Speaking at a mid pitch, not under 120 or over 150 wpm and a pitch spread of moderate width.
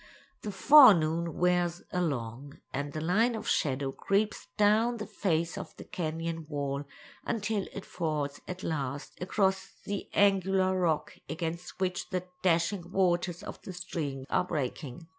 Yes: medium, 175 Hz; average, 140 wpm; average, 3.7 semitones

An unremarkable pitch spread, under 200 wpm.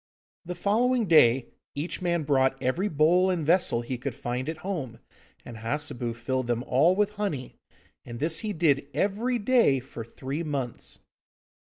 No: wide, 6.3 semitones; average, 160 wpm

